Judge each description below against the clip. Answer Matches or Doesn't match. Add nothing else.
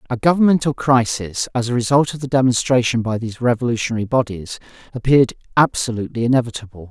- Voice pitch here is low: Matches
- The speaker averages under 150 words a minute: Matches